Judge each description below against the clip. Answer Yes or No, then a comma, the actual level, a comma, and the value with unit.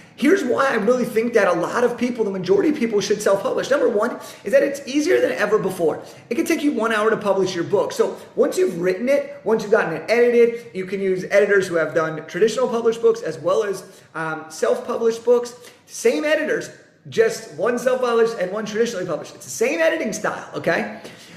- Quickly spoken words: Yes, fast, 220 wpm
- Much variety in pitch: Yes, wide, 5.8 semitones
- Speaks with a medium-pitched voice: No, high, 230 Hz